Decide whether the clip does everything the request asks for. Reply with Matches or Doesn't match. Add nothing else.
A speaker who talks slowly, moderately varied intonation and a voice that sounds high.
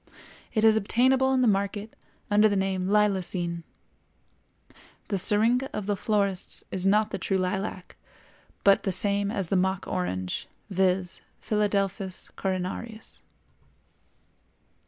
Doesn't match